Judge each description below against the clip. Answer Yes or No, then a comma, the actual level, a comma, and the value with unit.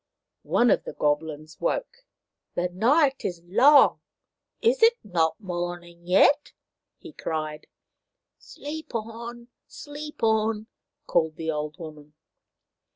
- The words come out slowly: Yes, slow, 130 wpm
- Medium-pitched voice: No, high, 205 Hz